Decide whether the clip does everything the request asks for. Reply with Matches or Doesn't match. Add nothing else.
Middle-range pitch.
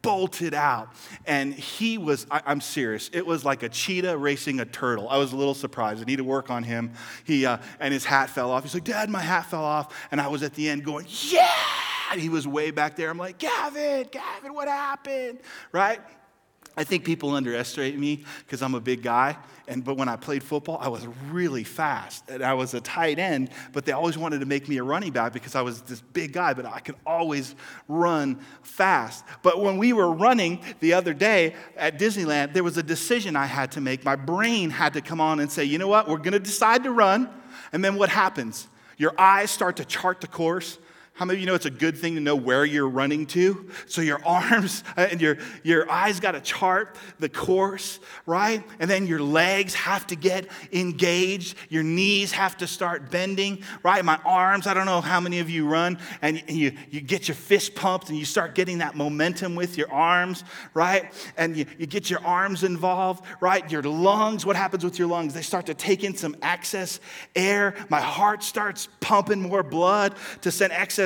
Matches